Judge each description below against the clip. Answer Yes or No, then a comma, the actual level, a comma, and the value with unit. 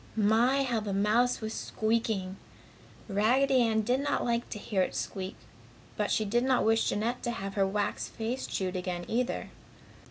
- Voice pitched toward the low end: No, high, 220 Hz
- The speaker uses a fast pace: No, average, 170 wpm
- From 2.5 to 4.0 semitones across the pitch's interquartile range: Yes, average, 3.2 semitones